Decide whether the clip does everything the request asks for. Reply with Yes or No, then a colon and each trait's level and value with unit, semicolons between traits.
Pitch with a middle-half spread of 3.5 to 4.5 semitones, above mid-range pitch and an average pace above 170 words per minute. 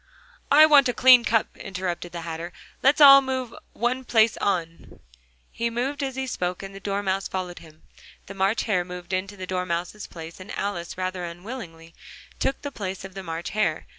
No: average, 5.2 semitones; high, 195 Hz; average, 185 wpm